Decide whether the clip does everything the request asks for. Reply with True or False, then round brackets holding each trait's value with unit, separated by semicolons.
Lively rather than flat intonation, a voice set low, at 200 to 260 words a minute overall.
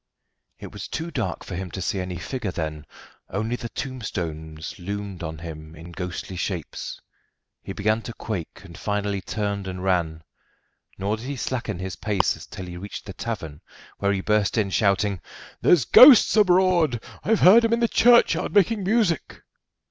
False (6.4 semitones; 100 Hz; 170 wpm)